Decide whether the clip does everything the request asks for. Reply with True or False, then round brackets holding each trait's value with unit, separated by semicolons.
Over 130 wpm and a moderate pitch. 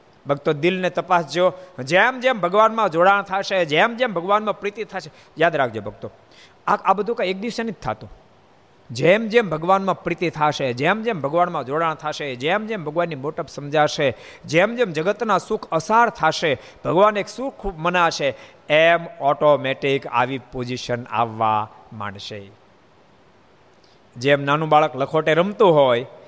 True (140 wpm; 165 Hz)